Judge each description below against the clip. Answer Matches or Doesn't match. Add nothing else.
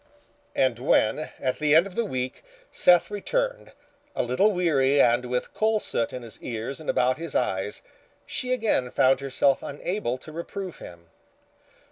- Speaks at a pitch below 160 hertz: Matches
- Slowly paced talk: Doesn't match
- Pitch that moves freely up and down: Matches